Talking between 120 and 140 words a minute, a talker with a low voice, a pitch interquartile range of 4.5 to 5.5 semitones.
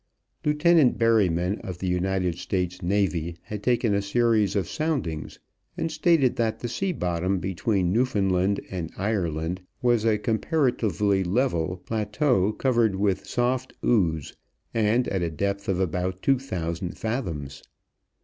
Yes: slow, 135 wpm; low, 100 Hz; average, 5.0 semitones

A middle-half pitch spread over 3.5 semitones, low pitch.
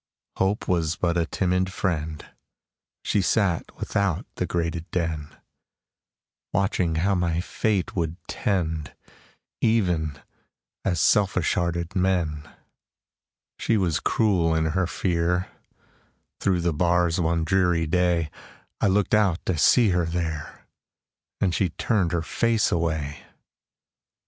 No: narrow, 2.5 semitones; very low, 85 Hz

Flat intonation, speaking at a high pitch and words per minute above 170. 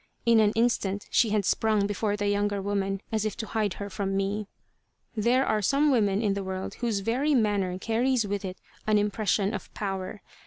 Yes: narrow, 2.1 semitones; high, 205 Hz; average, 195 wpm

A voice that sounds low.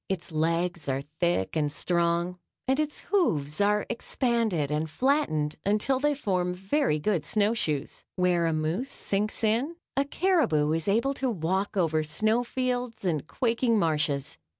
No: high, 190 Hz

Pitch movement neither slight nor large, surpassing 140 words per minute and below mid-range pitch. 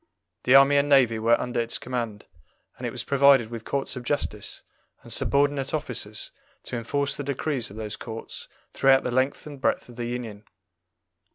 Yes: average, 3.2 semitones; average, 180 wpm; low, 125 Hz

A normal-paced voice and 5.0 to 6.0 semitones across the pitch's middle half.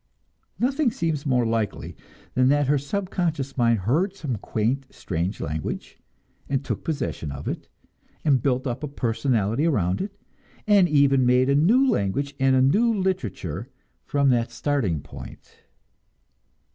Yes: average, 145 wpm; average, 5.3 semitones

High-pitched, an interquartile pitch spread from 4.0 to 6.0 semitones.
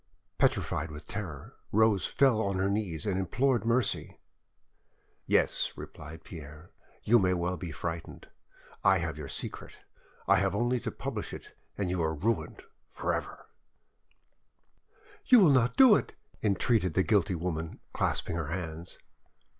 No: very low, 95 Hz; average, 5.1 semitones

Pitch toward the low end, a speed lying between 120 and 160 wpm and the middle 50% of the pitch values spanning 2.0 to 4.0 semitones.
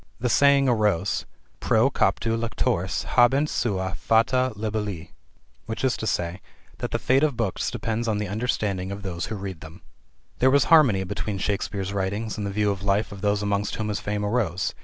No: low, 105 Hz; average, 175 wpm; average, 3.1 semitones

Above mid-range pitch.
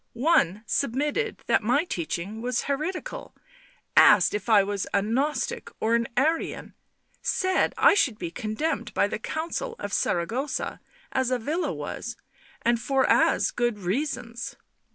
Yes: high, 245 Hz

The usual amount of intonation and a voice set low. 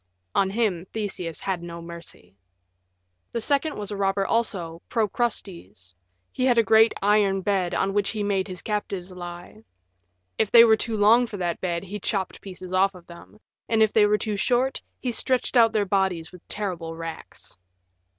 No: average, 3.7 semitones; high, 195 Hz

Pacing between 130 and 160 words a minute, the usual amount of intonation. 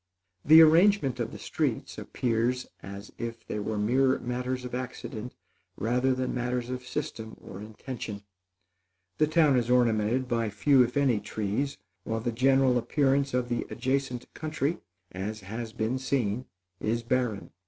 Yes: average, 150 wpm; average, 3.0 semitones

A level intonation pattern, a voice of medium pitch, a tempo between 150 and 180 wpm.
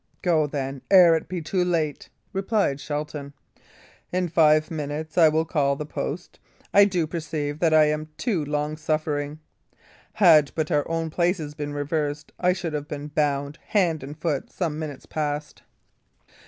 Yes: narrow, 2.2 semitones; medium, 155 Hz; average, 155 wpm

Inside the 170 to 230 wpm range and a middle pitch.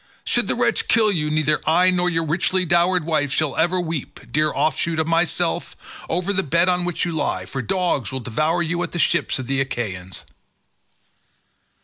Yes: average, 190 wpm; medium, 165 Hz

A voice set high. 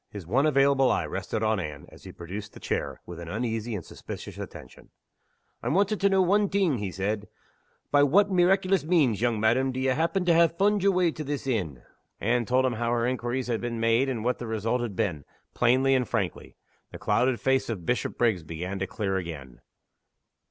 No: low, 120 Hz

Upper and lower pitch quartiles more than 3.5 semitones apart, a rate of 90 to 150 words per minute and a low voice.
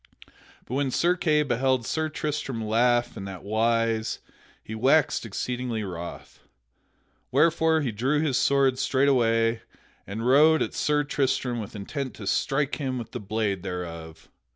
Yes: average, 4.3 semitones; average, 145 wpm; low, 125 Hz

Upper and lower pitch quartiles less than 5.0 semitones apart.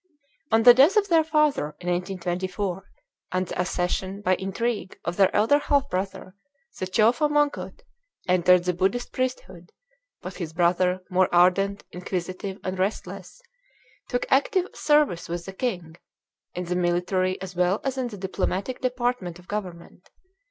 No: average, 5.3 semitones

